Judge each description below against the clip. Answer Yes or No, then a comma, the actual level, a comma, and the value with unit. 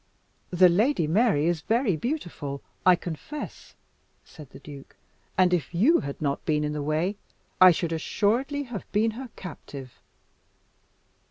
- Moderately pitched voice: Yes, medium, 175 Hz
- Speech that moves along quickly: No, average, 145 wpm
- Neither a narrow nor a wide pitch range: No, wide, 6.7 semitones